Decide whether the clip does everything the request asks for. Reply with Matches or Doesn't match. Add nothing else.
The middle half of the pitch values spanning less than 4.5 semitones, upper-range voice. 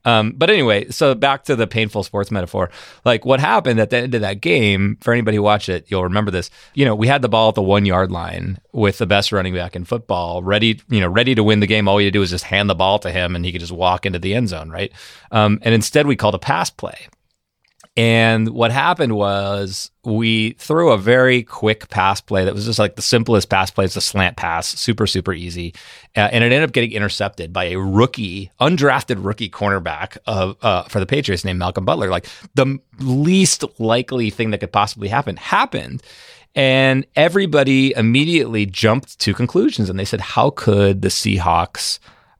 Doesn't match